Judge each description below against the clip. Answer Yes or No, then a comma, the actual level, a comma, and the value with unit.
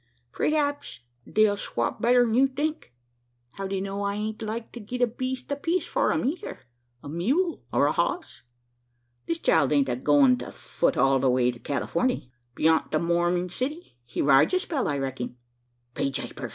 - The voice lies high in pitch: Yes, high, 200 Hz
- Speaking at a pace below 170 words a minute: No, average, 180 wpm